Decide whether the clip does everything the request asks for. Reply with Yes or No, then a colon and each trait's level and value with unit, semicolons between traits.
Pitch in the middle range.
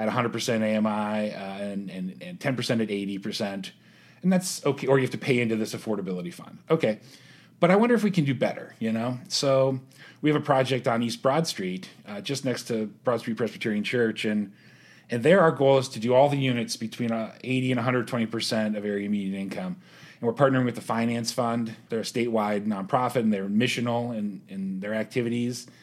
No: low, 120 Hz